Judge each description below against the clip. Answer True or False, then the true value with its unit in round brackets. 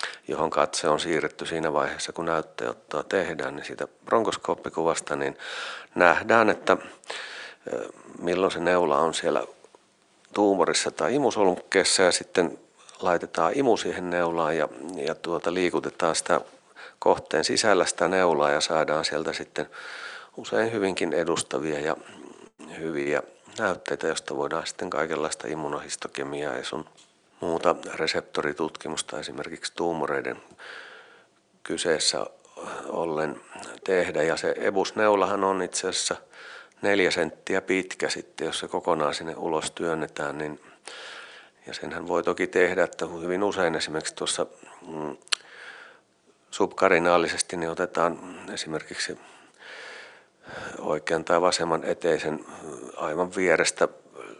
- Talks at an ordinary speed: False (110 wpm)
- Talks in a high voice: False (90 Hz)